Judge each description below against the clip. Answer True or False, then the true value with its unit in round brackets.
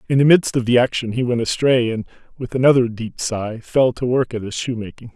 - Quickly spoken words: True (235 wpm)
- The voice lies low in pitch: True (120 Hz)